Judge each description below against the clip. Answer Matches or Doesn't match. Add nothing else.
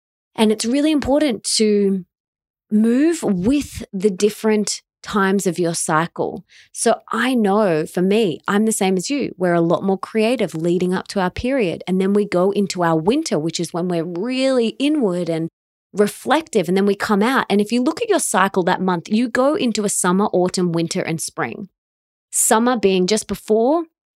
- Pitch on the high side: Matches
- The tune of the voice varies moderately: Matches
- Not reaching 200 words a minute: Matches